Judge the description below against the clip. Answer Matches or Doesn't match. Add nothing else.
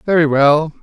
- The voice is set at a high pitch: Doesn't match